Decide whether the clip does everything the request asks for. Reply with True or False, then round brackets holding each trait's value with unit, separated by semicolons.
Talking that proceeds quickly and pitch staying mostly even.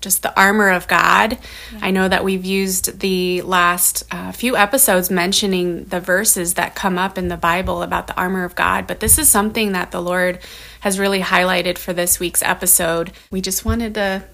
False (195 wpm; 1.5 semitones)